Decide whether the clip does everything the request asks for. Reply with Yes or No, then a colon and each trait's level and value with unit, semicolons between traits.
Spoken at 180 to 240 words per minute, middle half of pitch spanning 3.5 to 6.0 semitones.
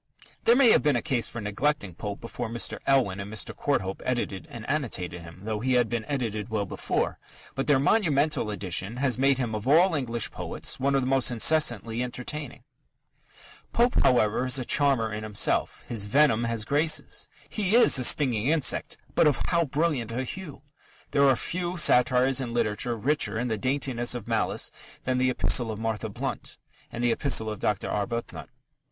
Yes: average, 185 wpm; average, 4.2 semitones